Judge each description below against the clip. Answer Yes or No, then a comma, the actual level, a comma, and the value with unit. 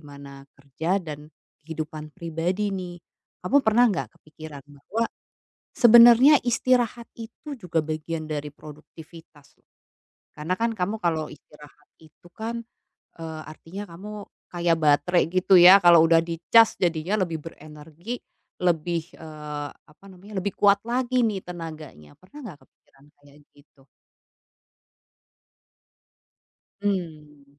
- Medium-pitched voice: Yes, medium, 165 Hz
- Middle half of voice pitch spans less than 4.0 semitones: No, average, 4.9 semitones